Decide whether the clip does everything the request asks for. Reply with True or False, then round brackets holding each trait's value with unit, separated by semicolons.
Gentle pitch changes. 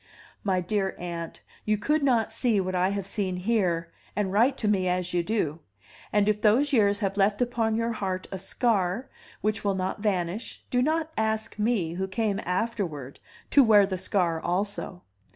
False (3.4 semitones)